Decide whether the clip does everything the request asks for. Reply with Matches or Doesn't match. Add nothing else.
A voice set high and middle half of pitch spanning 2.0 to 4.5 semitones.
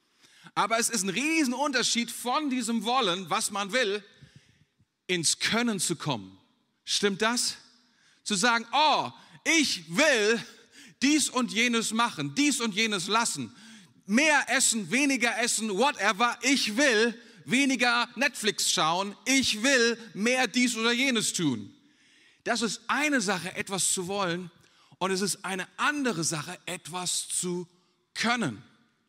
Doesn't match